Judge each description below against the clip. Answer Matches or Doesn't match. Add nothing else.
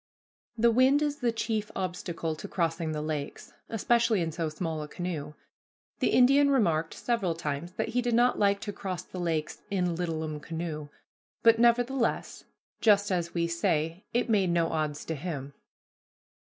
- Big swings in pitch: Matches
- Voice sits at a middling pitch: Matches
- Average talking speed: Matches